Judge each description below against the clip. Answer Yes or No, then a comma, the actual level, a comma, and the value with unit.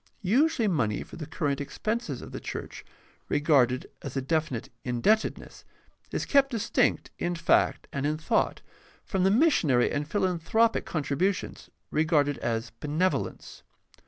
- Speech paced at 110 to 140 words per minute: Yes, slow, 135 wpm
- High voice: No, medium, 160 Hz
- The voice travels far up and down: Yes, wide, 6.1 semitones